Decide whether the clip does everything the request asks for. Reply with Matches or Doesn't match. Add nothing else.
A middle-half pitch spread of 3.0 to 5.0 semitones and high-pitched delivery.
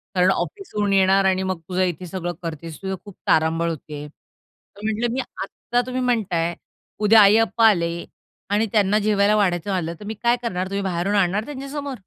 Matches